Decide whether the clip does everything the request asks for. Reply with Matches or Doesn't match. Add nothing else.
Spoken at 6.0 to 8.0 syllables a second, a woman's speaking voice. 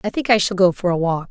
Matches